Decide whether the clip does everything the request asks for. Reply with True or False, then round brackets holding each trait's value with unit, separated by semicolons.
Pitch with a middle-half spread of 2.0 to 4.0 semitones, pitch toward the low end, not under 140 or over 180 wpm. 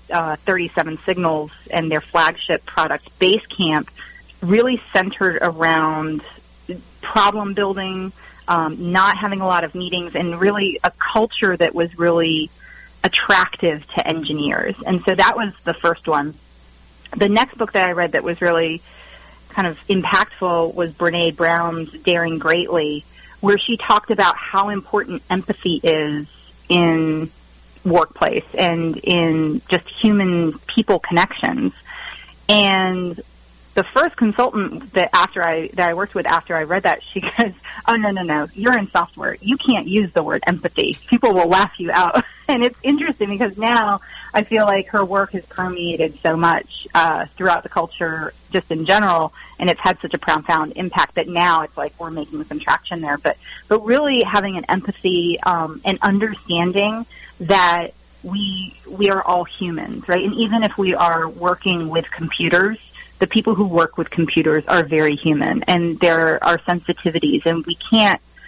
False (3.5 semitones; 175 Hz; 160 wpm)